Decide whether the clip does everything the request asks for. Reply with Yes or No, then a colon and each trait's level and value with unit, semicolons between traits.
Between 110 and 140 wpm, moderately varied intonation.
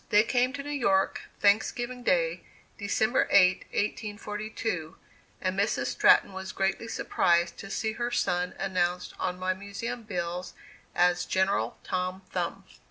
Yes: slow, 135 wpm; average, 3.2 semitones